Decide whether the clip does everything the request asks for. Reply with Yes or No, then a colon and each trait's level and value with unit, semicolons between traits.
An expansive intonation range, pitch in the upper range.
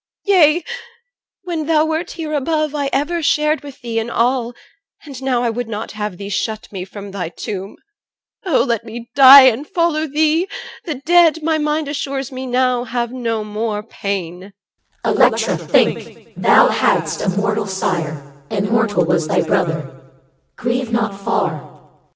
Yes: wide, 6.7 semitones; high, 240 Hz